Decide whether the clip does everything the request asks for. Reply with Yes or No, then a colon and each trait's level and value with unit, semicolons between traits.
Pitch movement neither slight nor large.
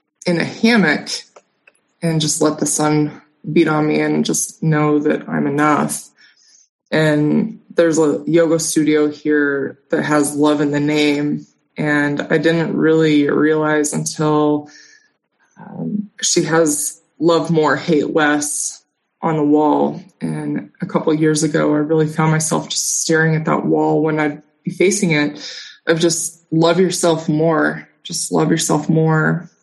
No: narrow, 1.7 semitones